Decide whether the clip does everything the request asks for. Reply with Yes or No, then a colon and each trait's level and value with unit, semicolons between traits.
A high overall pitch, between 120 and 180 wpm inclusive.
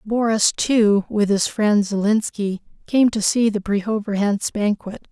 Yes: high, 210 Hz; average, 140 wpm